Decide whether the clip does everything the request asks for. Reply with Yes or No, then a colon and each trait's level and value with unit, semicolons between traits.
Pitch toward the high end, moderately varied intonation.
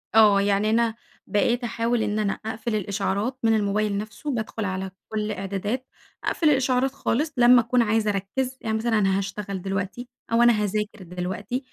Yes: high, 215 Hz; average, 3.1 semitones